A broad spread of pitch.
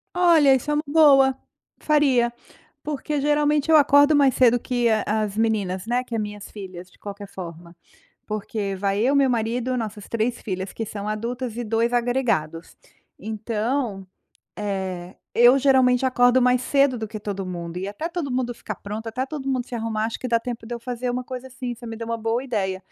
No: average, 3.8 semitones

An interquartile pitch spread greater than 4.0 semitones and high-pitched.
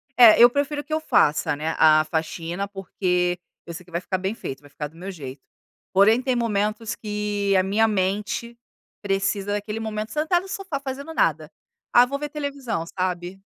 Yes: average, 5.2 semitones; high, 205 Hz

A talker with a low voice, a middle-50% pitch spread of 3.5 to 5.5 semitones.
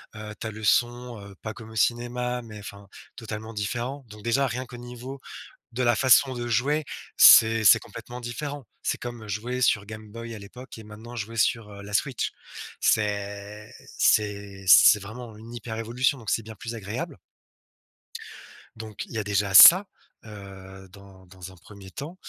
No: low, 110 Hz; average, 2.9 semitones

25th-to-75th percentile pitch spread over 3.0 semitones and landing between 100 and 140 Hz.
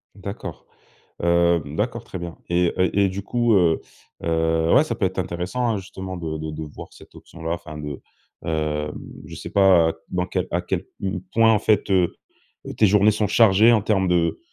No: average, 3.6 semitones; very low, 90 Hz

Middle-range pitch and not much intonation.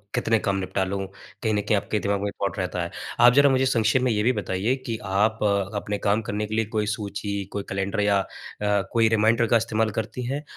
No: low, 105 Hz; narrow, 2.2 semitones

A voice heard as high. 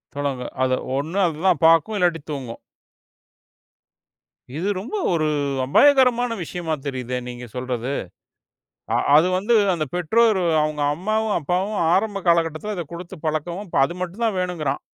No: medium, 170 Hz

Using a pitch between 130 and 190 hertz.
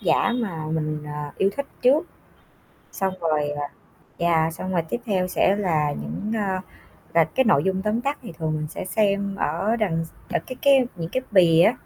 Yes: medium, 185 Hz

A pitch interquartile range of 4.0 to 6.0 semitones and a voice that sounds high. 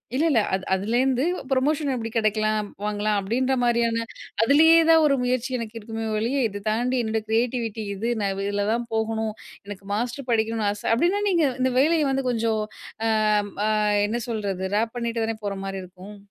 No: average, 3.2 semitones; high, 230 Hz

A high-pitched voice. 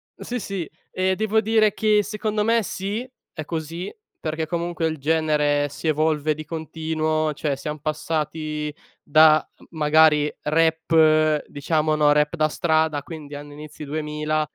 No: medium, 155 Hz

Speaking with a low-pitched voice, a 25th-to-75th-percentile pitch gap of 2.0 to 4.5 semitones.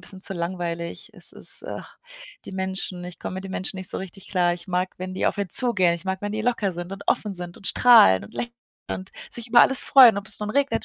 No: high, 190 Hz; average, 2.9 semitones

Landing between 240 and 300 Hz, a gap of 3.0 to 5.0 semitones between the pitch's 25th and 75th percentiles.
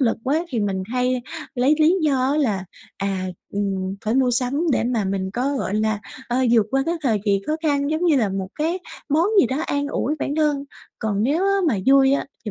No: very high, 255 Hz; wide, 5.5 semitones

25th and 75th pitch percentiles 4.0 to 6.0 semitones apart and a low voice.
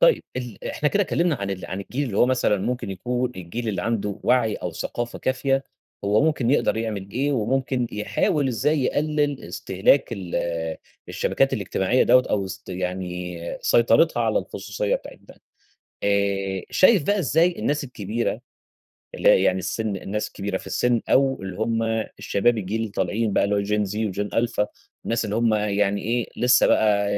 Yes: average, 4.3 semitones; low, 110 Hz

